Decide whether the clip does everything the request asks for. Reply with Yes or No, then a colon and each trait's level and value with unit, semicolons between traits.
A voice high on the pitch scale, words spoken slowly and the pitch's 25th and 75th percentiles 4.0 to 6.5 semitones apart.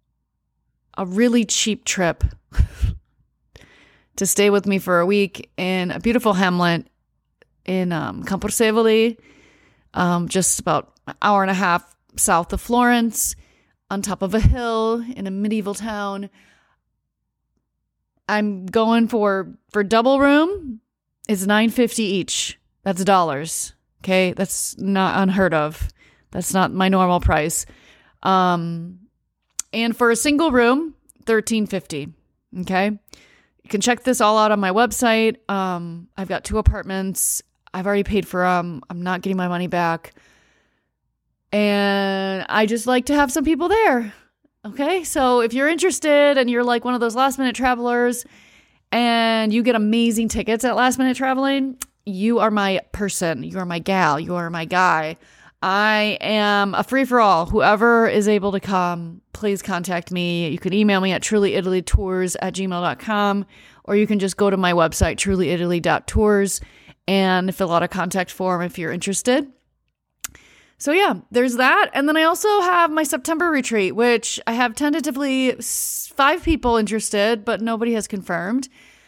No: high, 205 Hz; average, 150 wpm; average, 4.5 semitones